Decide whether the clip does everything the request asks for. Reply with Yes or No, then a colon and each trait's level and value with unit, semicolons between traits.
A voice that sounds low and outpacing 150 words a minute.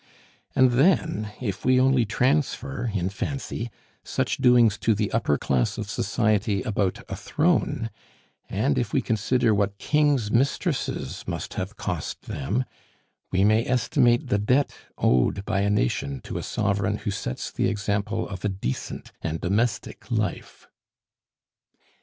No: low, 110 Hz; average, 140 wpm